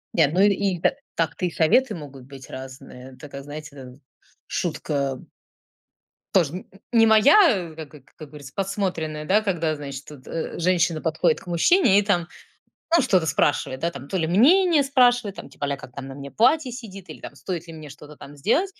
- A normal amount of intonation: No, wide, 6.0 semitones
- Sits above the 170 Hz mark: No, medium, 165 Hz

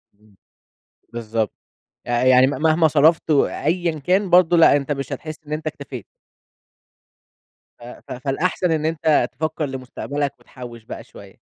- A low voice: No, medium, 145 Hz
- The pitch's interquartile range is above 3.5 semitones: Yes, average, 3.9 semitones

